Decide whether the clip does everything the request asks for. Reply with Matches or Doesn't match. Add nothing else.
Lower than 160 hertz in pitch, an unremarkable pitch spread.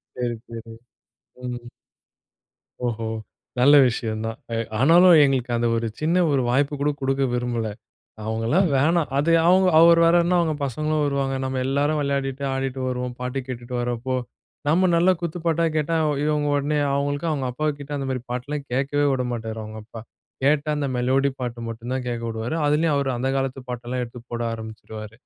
Matches